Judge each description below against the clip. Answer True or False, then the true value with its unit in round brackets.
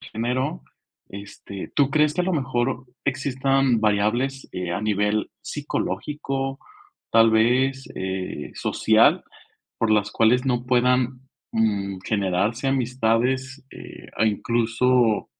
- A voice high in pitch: False (120 Hz)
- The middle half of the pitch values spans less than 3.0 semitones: False (3.7 semitones)